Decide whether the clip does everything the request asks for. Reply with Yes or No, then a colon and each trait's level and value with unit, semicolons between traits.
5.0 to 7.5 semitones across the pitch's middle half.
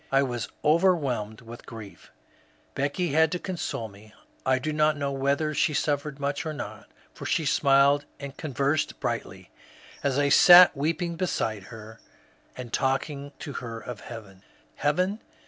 No: average, 4.1 semitones